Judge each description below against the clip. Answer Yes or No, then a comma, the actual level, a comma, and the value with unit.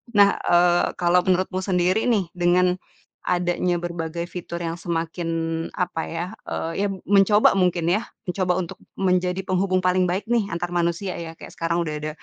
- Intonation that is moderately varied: No, narrow, 1.6 semitones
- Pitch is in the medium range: Yes, medium, 180 Hz